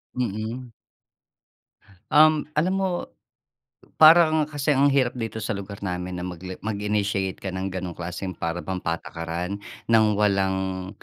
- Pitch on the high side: No, low, 100 Hz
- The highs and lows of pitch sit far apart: Yes, wide, 5.8 semitones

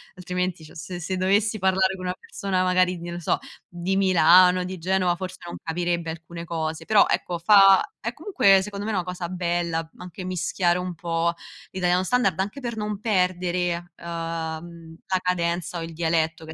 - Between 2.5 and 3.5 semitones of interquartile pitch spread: No, narrow, 1.8 semitones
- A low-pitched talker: No, medium, 180 Hz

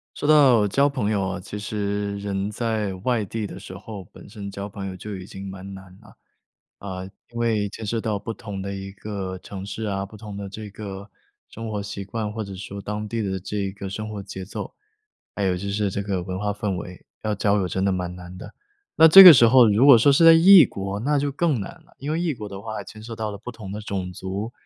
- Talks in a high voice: No, low, 100 Hz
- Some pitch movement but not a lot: No, narrow, 2.3 semitones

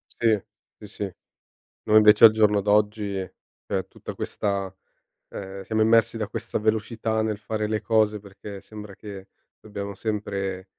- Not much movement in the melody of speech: Yes, narrow, 1.5 semitones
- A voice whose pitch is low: Yes, low, 105 Hz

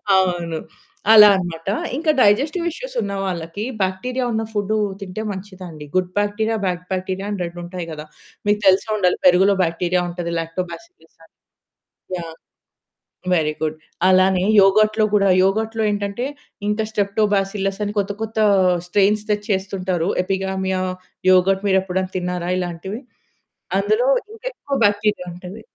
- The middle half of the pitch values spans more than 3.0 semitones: No, average, 2.7 semitones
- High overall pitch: Yes, high, 195 Hz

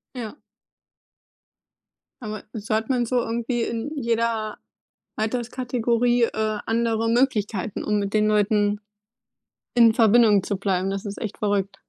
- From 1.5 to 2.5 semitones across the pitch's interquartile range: Yes, narrow, 2.2 semitones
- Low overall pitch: No, high, 220 Hz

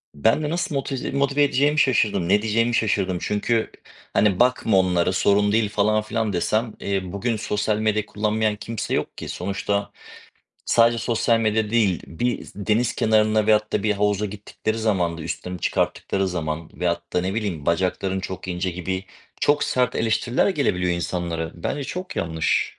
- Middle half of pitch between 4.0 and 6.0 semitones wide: No, average, 3.6 semitones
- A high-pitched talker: No, low, 105 Hz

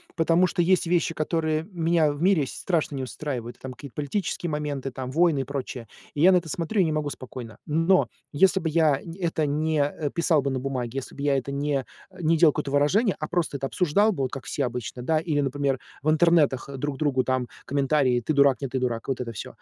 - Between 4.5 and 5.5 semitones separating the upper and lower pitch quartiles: No, average, 3.6 semitones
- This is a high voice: No, medium, 145 Hz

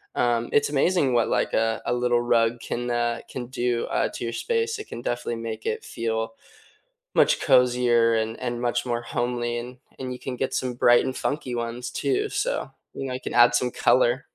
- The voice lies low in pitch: Yes, low, 120 Hz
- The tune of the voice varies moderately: No, narrow, 1.4 semitones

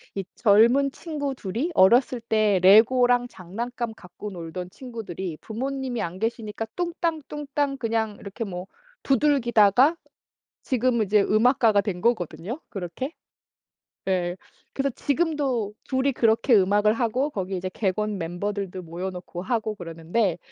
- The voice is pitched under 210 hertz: No, high, 220 Hz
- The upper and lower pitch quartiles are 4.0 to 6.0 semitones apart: Yes, average, 5.1 semitones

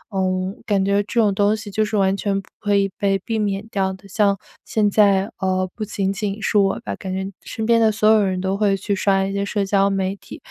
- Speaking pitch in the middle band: No, high, 200 Hz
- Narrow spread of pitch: Yes, narrow, 1.4 semitones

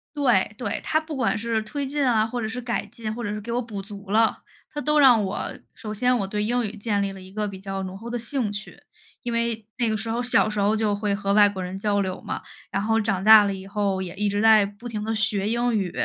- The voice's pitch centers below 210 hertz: No, high, 215 Hz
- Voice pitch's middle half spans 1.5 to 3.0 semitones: Yes, narrow, 2.6 semitones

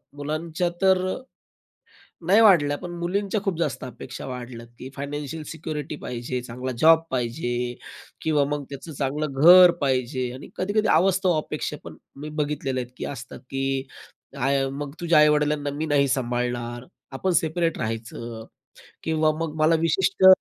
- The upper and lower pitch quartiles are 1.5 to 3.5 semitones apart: No, average, 4.2 semitones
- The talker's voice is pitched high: No, medium, 145 Hz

